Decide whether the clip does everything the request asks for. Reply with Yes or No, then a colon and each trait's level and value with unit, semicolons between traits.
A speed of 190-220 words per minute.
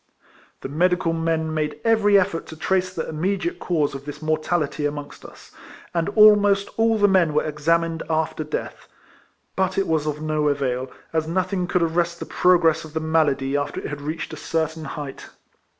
No: average, 180 wpm